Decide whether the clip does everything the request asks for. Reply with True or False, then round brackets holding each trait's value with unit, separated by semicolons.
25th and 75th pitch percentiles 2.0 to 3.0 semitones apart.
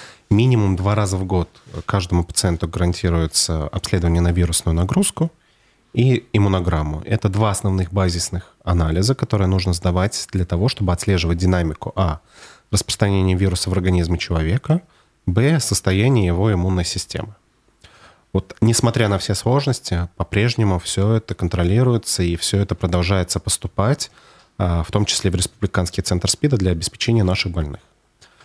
False (3.8 semitones)